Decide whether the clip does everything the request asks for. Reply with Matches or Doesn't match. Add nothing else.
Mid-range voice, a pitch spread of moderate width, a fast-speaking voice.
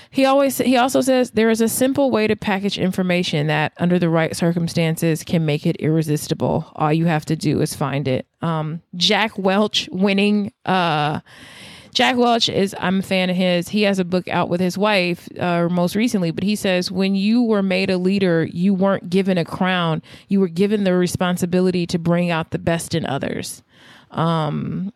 Doesn't match